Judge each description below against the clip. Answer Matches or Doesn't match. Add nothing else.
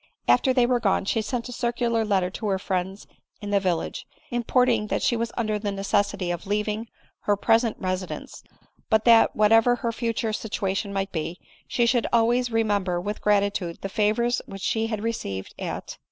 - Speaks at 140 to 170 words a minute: Doesn't match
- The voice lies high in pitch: Matches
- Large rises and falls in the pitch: Doesn't match